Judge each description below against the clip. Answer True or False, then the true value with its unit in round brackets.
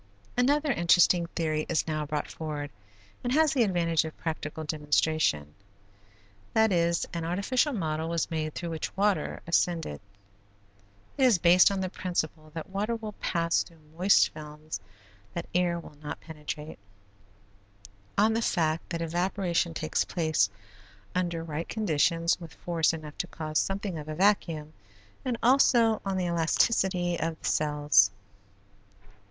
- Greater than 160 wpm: False (145 wpm)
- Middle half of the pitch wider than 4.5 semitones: False (3.6 semitones)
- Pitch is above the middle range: False (170 Hz)